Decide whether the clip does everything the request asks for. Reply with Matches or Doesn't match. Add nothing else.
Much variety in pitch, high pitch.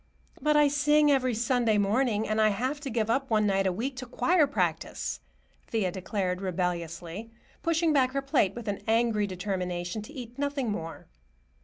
Matches